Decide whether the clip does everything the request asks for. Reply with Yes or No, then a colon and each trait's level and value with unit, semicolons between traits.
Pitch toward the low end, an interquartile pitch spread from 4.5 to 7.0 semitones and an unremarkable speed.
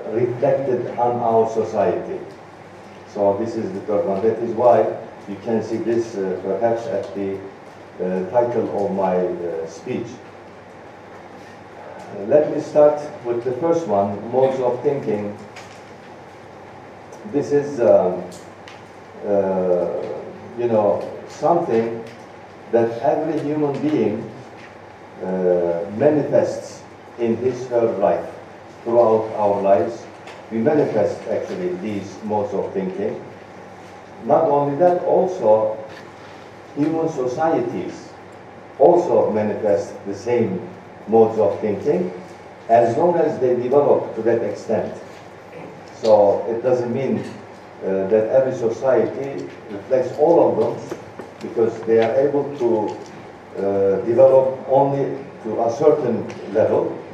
Yes: low, 115 Hz; average, 5.2 semitones; average, 115 wpm